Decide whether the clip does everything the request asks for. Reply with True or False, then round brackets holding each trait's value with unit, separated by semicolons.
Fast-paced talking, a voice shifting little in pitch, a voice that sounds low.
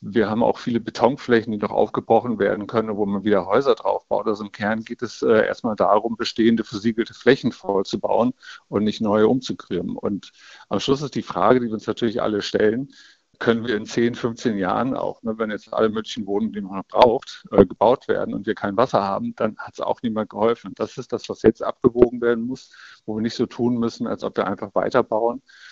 True (220 wpm; 1.8 semitones; 115 Hz)